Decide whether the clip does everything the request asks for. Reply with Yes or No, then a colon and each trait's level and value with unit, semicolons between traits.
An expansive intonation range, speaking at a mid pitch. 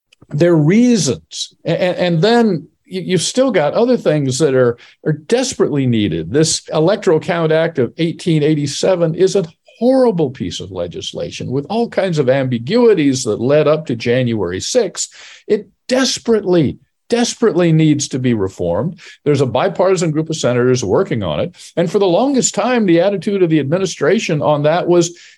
Yes: wide, 5.8 semitones; medium, 170 Hz